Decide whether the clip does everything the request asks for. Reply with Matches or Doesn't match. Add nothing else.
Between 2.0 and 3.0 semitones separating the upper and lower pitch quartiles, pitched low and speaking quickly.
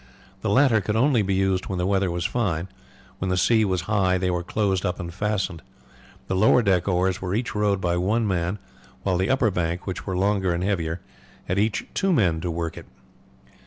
Matches